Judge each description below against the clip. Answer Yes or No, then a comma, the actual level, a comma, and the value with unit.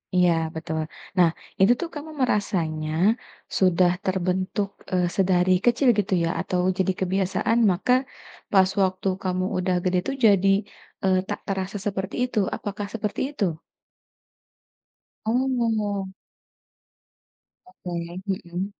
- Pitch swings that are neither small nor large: No, narrow, 2.3 semitones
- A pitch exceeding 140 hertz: Yes, high, 190 Hz